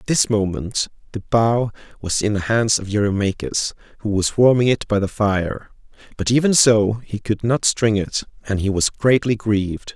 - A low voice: Yes, low, 105 Hz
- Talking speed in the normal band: Yes, average, 185 wpm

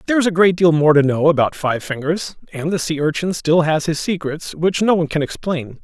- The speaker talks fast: Yes, fast, 245 wpm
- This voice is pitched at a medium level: Yes, medium, 160 Hz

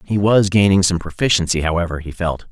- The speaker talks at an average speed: Yes, average, 190 wpm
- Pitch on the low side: Yes, very low, 95 Hz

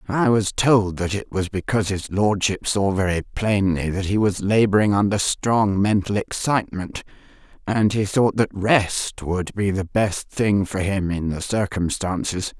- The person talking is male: No, female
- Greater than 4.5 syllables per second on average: No, 4.3 syllables/s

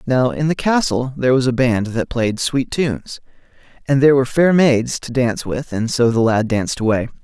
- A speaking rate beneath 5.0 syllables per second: No, 5.4 syllables/s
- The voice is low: Yes, low, 125 Hz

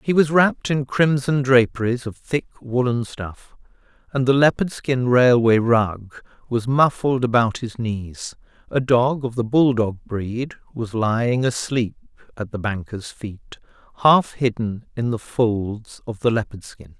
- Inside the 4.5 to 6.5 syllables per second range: No, 4.1 syllables/s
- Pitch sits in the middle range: No, low, 120 Hz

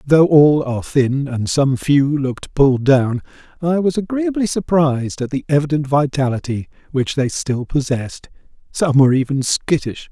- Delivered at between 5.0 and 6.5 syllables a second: No, 4.8 syllables/s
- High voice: No, medium, 140 Hz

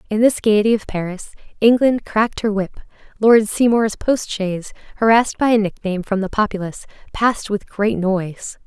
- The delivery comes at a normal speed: Yes, average, 165 wpm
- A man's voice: No, female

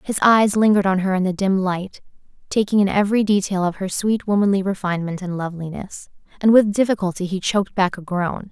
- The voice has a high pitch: Yes, high, 195 Hz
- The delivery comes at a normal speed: Yes, average, 195 wpm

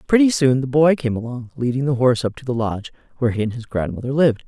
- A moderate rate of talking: No, fast, 255 wpm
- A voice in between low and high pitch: No, low, 130 Hz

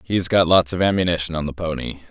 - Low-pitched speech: Yes, very low, 85 Hz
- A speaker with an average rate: No, fast, 230 wpm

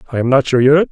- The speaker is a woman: No, male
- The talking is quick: Yes, fast, 330 wpm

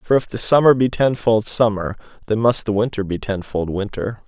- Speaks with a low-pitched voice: Yes, low, 110 Hz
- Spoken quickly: No, average, 195 wpm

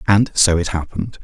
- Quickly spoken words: No, average, 195 wpm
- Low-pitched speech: Yes, very low, 95 Hz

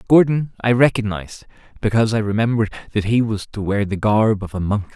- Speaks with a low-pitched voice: Yes, low, 110 Hz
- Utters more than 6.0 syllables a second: Yes, 6.2 syllables/s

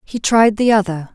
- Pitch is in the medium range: No, high, 210 Hz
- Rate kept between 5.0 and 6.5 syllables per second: No, 4.8 syllables/s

